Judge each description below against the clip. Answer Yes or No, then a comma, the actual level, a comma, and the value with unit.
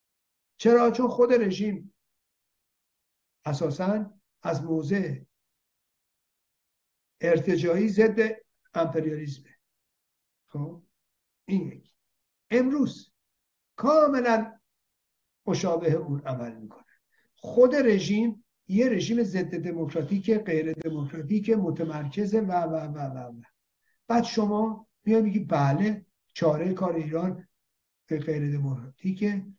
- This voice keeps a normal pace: No, slow, 85 wpm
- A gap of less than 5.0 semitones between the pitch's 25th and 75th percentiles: No, wide, 5.6 semitones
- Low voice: No, medium, 185 Hz